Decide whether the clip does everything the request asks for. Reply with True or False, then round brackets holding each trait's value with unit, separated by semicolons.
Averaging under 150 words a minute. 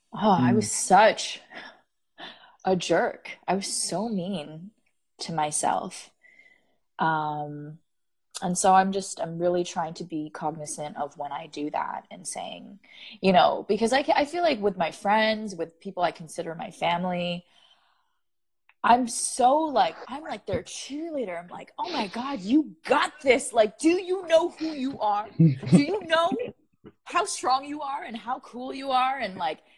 False (160 wpm)